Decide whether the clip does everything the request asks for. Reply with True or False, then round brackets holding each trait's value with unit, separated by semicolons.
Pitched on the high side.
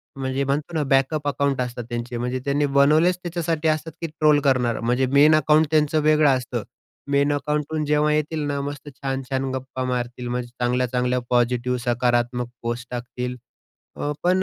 False (135 Hz)